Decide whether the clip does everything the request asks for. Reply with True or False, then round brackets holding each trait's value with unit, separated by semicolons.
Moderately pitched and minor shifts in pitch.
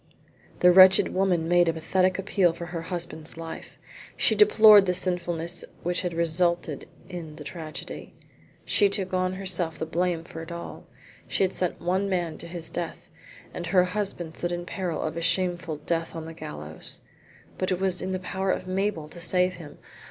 True (175 Hz; 2.1 semitones)